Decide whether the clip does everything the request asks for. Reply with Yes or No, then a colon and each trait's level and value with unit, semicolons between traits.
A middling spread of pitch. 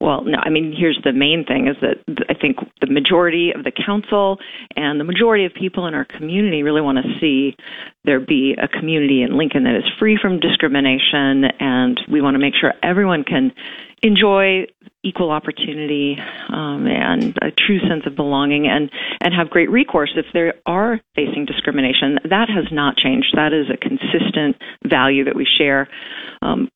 No: wide, 5.8 semitones